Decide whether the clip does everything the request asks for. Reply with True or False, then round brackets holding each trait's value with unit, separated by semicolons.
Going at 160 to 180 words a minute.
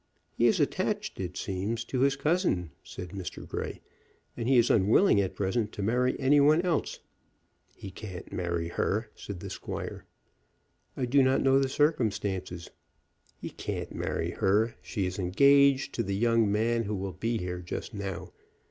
True (165 wpm)